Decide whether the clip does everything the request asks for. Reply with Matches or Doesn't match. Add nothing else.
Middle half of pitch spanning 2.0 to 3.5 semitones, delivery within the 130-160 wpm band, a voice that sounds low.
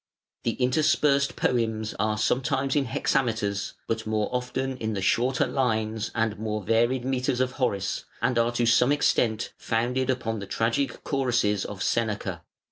Matches